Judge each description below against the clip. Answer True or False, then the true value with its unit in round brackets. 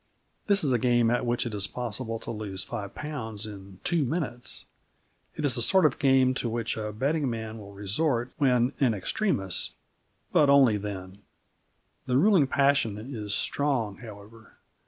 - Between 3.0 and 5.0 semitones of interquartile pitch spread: True (4.7 semitones)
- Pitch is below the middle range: True (120 Hz)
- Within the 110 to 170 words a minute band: True (165 wpm)